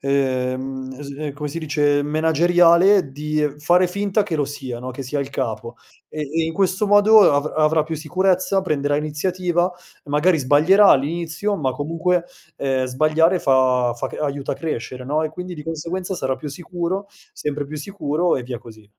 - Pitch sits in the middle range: Yes, medium, 150 Hz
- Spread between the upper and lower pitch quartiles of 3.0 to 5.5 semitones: Yes, average, 4.2 semitones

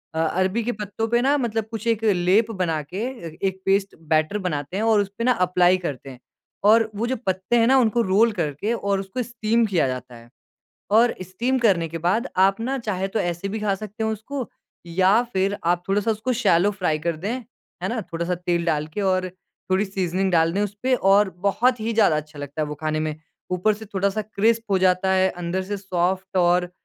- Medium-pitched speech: No, high, 195 Hz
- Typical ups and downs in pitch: Yes, average, 3.8 semitones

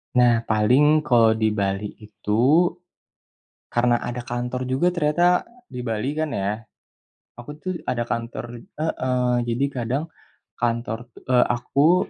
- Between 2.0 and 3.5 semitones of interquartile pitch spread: No, average, 3.9 semitones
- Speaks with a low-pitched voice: Yes, low, 125 Hz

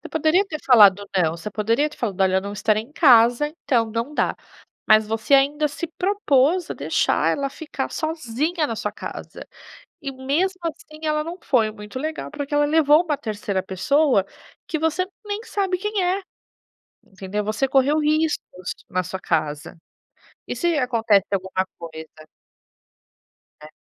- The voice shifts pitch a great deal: Yes, wide, 6.9 semitones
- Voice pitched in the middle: No, very high, 270 Hz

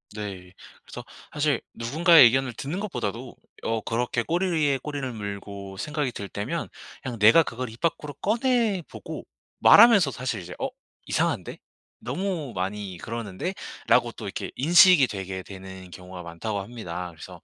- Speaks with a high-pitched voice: No, low, 120 Hz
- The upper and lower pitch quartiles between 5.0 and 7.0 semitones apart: No, wide, 7.7 semitones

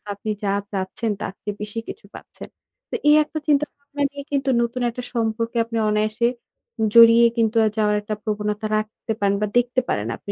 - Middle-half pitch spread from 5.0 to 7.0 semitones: No, narrow, 2.6 semitones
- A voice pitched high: Yes, high, 225 Hz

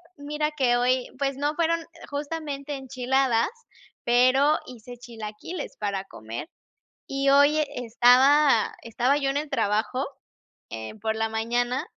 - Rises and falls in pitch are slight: No, average, 3.6 semitones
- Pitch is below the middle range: No, very high, 260 Hz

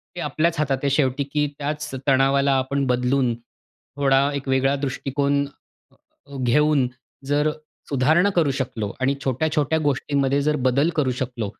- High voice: No, medium, 140 Hz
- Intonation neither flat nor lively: No, narrow, 1.9 semitones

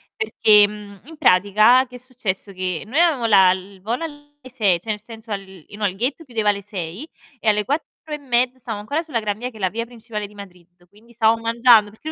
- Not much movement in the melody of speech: No, average, 3.7 semitones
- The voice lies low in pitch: No, high, 220 Hz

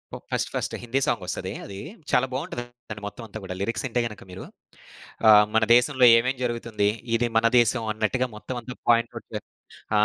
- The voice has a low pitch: Yes, low, 115 Hz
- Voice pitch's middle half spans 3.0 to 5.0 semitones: No, narrow, 2.4 semitones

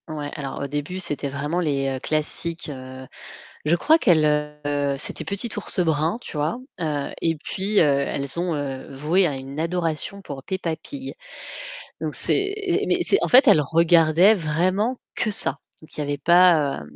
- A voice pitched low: No, medium, 155 Hz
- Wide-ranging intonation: No, average, 4.0 semitones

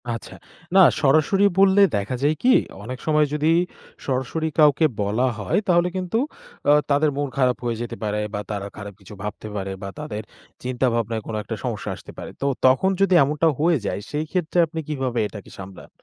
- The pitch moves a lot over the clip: Yes, wide, 6.5 semitones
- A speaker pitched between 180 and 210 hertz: No, low, 135 Hz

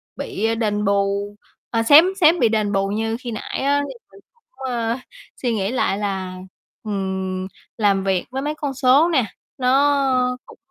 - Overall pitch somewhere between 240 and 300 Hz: No, high, 225 Hz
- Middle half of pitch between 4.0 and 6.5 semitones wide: Yes, average, 5.1 semitones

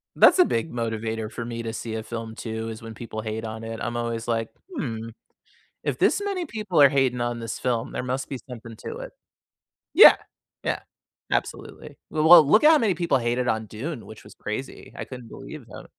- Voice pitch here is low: Yes, low, 115 Hz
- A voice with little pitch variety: No, average, 3.1 semitones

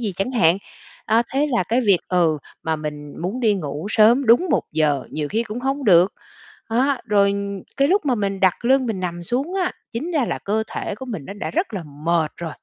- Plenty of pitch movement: Yes, wide, 6.5 semitones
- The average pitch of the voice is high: Yes, high, 210 Hz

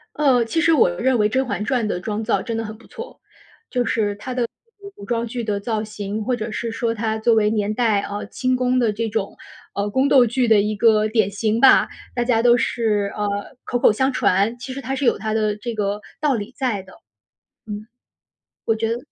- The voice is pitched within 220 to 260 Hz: Yes, high, 225 Hz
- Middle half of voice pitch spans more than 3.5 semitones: No, average, 2.9 semitones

